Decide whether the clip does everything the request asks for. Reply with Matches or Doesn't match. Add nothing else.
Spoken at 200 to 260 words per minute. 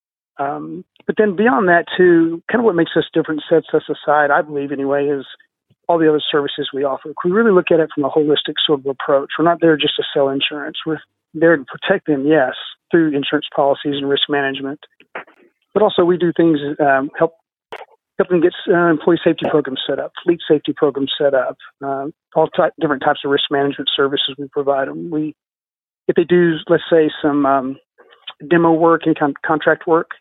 Matches